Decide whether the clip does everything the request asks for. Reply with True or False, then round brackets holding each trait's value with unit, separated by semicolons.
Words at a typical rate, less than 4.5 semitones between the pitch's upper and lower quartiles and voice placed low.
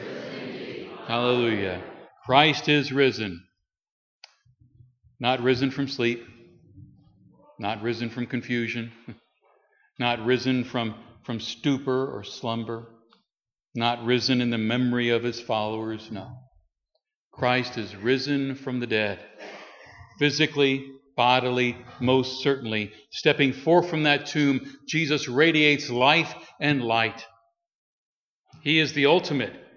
False (105 wpm; 3.2 semitones; 125 Hz)